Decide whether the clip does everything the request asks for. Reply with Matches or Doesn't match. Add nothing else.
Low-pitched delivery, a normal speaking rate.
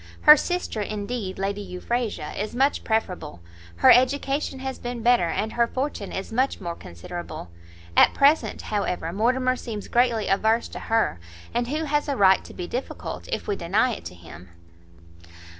Doesn't match